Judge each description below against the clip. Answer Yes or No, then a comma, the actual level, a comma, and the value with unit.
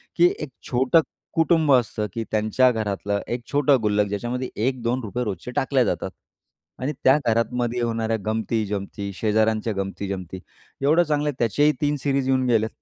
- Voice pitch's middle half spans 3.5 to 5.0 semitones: Yes, average, 3.8 semitones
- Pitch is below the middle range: Yes, low, 120 Hz